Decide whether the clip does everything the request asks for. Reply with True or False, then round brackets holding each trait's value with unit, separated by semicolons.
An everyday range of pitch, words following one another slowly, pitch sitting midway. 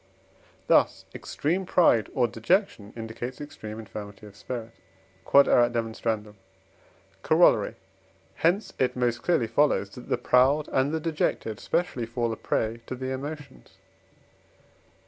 False (4.3 semitones; 120 wpm; 125 Hz)